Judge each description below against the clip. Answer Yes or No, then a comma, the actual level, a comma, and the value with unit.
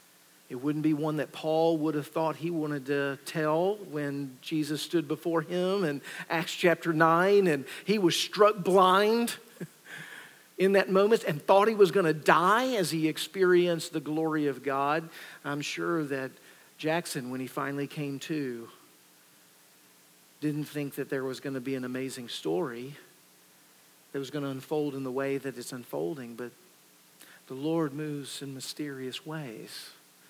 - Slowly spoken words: No, average, 160 wpm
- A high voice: No, medium, 150 Hz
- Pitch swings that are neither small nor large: Yes, average, 3.8 semitones